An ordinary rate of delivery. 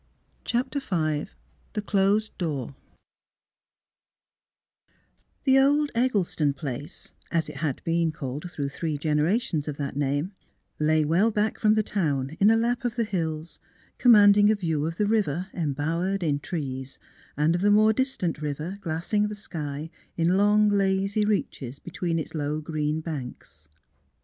Yes: average, 150 wpm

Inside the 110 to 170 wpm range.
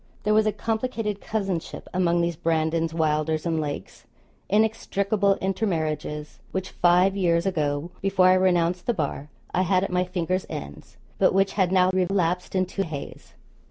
Yes: average, 155 wpm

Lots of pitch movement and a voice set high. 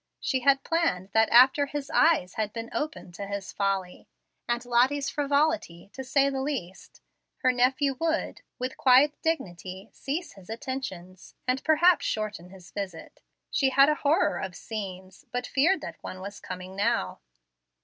Yes: wide, 6.6 semitones; high, 245 Hz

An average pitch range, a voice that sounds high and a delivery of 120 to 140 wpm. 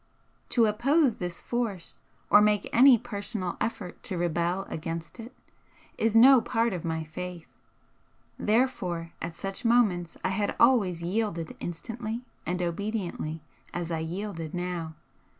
Yes: average, 5.0 semitones; high, 195 Hz; slow, 135 wpm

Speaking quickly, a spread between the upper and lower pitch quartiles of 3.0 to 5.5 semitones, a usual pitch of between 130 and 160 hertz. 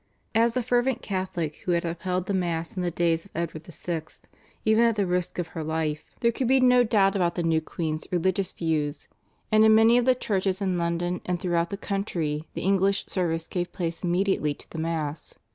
No: fast, 210 wpm; average, 3.4 semitones; medium, 180 Hz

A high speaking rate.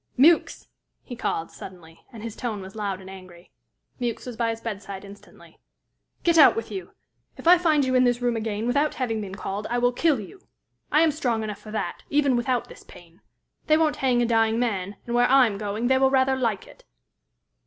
Yes: fast, 215 wpm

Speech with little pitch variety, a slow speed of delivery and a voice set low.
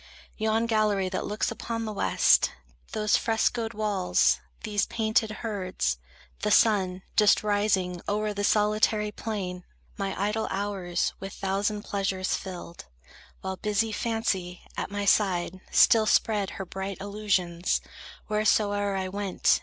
No: narrow, 2.1 semitones; slow, 130 wpm; high, 205 Hz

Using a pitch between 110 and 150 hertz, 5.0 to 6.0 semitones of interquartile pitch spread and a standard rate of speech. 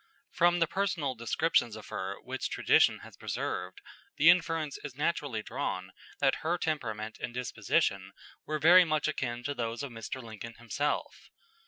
Yes: medium, 140 Hz; wide, 5.5 semitones; average, 155 wpm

